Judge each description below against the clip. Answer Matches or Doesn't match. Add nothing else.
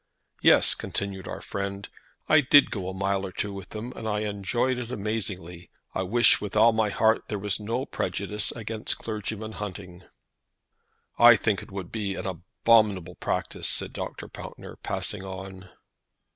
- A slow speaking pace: Doesn't match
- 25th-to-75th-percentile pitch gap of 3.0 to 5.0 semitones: Doesn't match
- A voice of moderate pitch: Doesn't match